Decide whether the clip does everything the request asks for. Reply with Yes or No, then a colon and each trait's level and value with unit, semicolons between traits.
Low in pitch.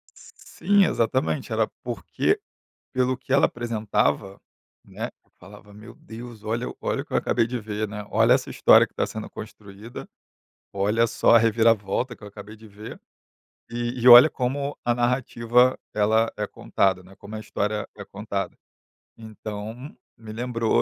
Yes: low, 110 Hz